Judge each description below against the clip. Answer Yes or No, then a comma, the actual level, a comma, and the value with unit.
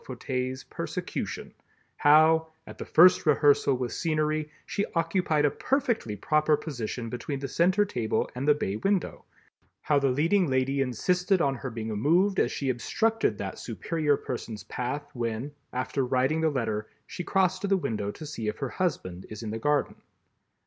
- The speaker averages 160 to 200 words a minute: Yes, average, 165 wpm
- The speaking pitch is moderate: Yes, medium, 145 Hz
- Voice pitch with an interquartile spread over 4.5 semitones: Yes, average, 5.1 semitones